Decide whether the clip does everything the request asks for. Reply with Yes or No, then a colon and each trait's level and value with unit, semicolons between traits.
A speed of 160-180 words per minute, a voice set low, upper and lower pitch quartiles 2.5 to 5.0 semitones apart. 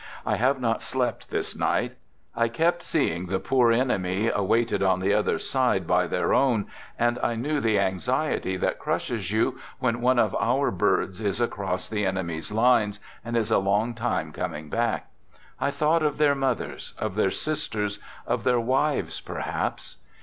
Yes: average, 170 wpm; low, 115 Hz; average, 4.4 semitones